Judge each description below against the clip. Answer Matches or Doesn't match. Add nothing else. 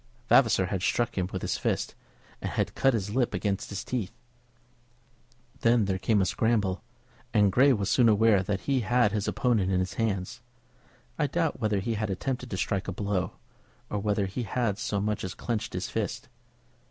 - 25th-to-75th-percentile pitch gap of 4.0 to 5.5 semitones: Doesn't match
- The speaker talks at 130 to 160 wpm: Doesn't match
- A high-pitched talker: Doesn't match